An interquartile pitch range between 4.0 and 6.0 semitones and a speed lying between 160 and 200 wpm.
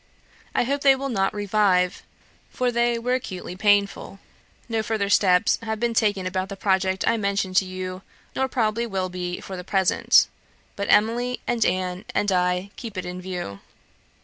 No: average, 3.6 semitones; average, 175 wpm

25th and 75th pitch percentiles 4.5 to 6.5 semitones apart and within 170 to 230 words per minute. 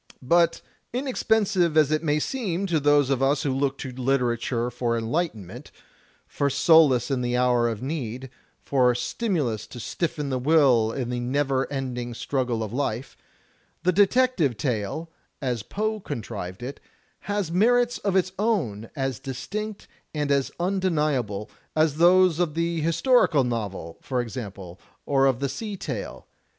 No: wide, 5.6 semitones; average, 150 wpm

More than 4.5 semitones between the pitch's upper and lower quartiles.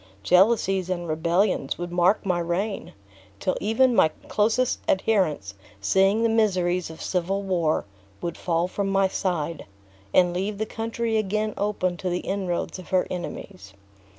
No: average, 3.1 semitones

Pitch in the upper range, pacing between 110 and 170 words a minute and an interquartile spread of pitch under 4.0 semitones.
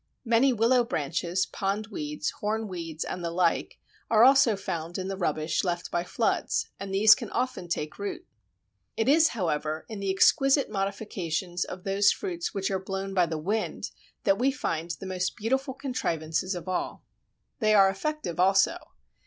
No: high, 195 Hz; average, 160 wpm; average, 4.6 semitones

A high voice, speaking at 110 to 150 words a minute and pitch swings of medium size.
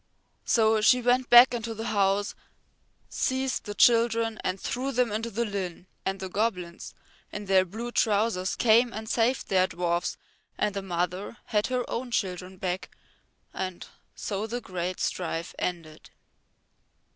Yes: high, 210 Hz; average, 145 wpm; average, 4.0 semitones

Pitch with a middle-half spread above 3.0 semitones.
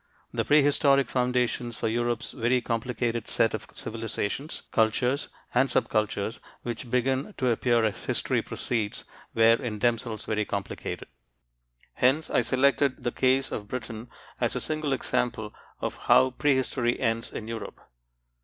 No: narrow, 2.5 semitones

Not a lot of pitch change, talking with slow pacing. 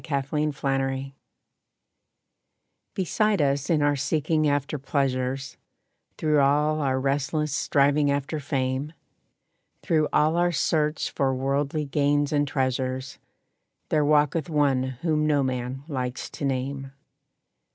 Yes: narrow, 2.1 semitones; slow, 115 wpm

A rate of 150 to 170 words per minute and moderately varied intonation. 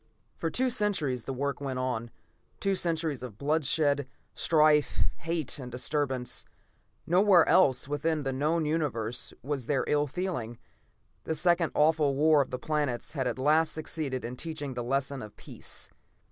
Yes: average, 160 wpm; average, 3.7 semitones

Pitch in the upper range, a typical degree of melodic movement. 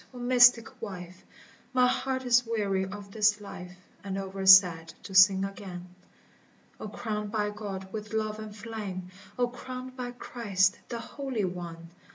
Yes: high, 210 Hz; average, 3.7 semitones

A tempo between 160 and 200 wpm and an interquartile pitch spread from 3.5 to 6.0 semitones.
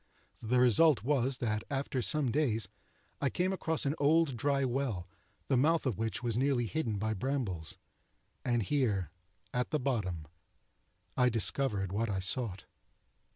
No: average, 150 wpm; average, 4.5 semitones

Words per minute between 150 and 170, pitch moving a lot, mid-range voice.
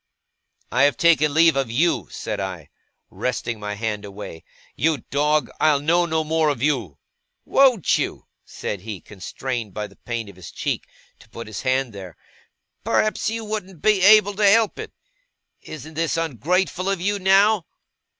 Yes: average, 165 wpm; wide, 8.5 semitones; medium, 150 Hz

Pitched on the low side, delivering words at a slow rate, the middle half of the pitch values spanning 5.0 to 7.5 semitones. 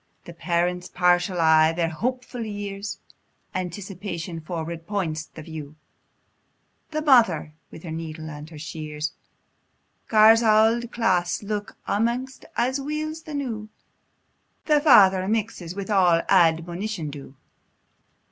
No: medium, 185 Hz; slow, 120 wpm; average, 5.3 semitones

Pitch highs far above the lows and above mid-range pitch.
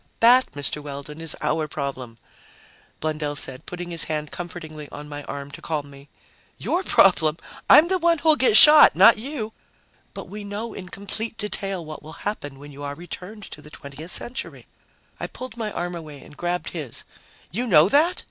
No: wide, 6.7 semitones; medium, 170 Hz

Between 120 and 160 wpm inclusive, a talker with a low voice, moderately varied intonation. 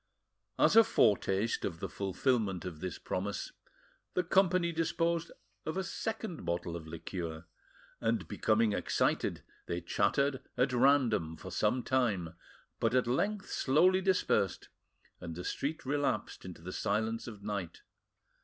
No: slow, 135 wpm; low, 115 Hz; wide, 8.0 semitones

